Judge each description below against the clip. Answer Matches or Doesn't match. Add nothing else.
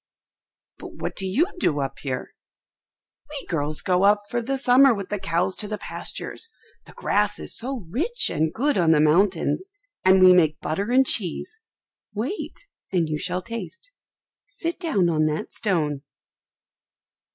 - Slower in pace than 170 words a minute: Matches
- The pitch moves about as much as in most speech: Doesn't match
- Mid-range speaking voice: Doesn't match